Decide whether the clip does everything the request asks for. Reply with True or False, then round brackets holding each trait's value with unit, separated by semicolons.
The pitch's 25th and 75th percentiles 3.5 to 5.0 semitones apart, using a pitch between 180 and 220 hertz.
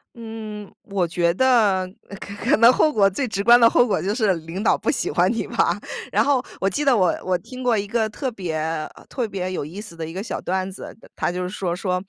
True (4.1 semitones; 200 Hz)